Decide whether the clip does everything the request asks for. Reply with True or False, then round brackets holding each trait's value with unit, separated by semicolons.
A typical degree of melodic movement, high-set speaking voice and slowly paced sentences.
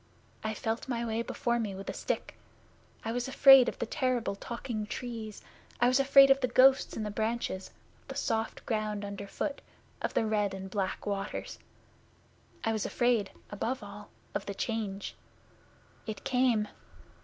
False (3.0 semitones; 225 Hz; 165 wpm)